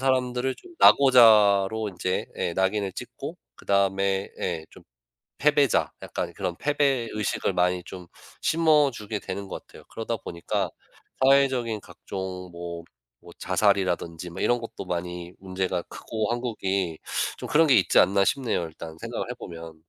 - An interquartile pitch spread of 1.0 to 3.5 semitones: No, average, 5.3 semitones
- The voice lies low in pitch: Yes, low, 100 Hz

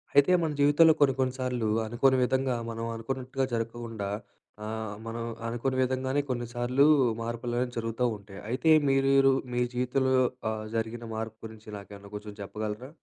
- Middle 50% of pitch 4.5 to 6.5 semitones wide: No, average, 2.8 semitones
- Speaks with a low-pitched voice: Yes, low, 120 Hz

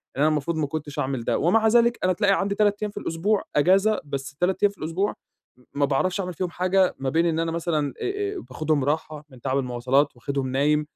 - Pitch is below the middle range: No, medium, 160 Hz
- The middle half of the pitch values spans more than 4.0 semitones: Yes, wide, 5.5 semitones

